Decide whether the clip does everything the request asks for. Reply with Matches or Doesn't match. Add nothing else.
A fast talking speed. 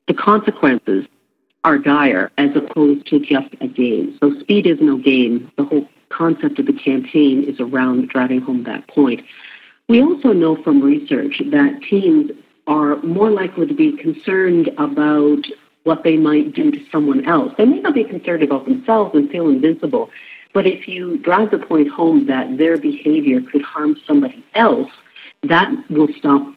Doesn't match